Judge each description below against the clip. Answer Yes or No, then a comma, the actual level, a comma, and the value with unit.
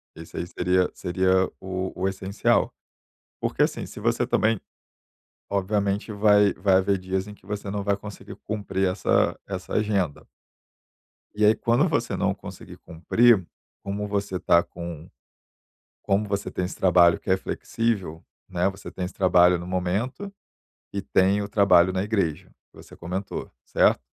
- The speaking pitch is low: Yes, very low, 95 Hz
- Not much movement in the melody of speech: Yes, narrow, 1.9 semitones